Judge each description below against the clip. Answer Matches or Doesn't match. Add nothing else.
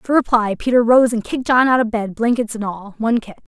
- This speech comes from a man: Doesn't match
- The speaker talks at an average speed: Doesn't match